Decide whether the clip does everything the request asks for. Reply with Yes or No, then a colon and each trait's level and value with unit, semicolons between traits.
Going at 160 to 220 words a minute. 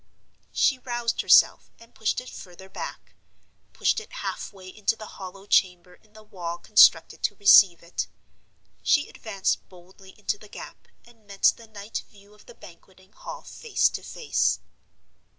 No: average, 150 wpm